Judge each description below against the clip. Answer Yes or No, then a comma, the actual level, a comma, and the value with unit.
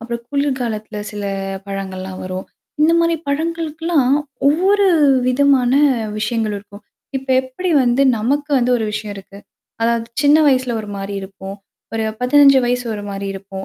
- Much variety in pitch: Yes, wide, 5.7 semitones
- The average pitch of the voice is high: Yes, high, 240 Hz